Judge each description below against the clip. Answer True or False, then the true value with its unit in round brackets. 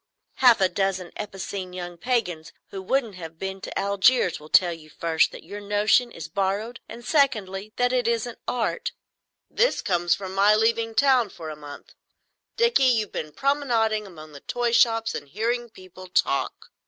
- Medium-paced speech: True (170 wpm)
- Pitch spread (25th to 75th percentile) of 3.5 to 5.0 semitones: True (4.7 semitones)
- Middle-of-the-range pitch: False (205 Hz)